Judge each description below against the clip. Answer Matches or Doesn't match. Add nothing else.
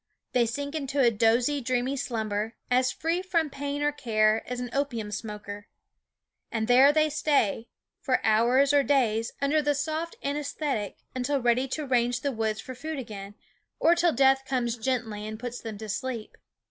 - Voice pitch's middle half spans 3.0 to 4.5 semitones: Matches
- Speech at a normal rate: Matches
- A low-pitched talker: Doesn't match